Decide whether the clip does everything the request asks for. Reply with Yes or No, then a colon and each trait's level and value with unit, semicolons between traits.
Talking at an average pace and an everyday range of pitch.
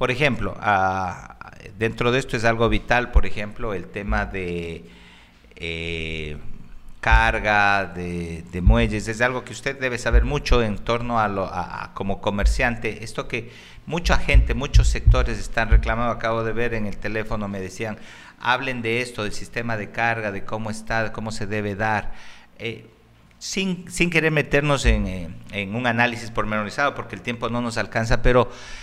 Yes: average, 170 wpm; average, 3.4 semitones